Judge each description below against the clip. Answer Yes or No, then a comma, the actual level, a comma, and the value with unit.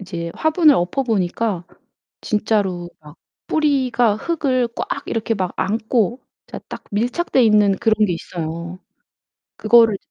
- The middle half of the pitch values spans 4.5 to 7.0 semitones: Yes, average, 5.1 semitones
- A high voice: Yes, high, 215 Hz